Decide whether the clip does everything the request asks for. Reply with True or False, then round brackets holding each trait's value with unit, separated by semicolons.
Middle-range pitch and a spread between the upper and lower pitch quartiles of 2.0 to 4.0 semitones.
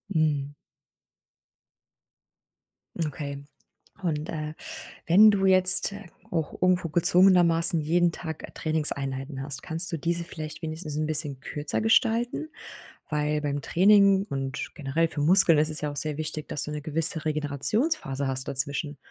True (155 Hz; 3.1 semitones)